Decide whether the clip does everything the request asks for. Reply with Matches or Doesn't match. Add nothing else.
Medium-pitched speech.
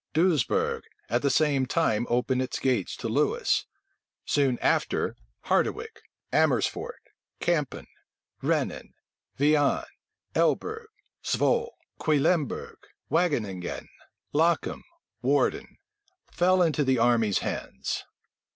Matches